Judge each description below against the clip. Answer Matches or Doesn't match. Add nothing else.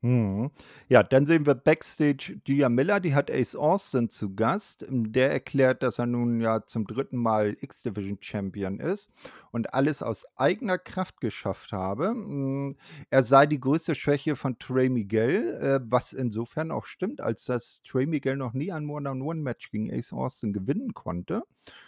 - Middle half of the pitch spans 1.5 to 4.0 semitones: Doesn't match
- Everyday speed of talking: Matches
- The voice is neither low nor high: Doesn't match